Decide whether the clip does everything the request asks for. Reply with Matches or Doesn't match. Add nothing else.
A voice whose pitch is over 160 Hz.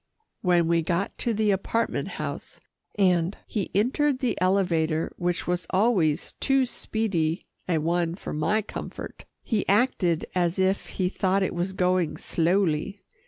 Matches